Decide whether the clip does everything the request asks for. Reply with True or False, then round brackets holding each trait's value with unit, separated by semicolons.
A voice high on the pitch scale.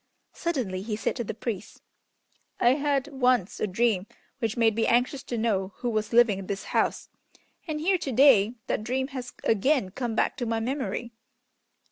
True (235 Hz)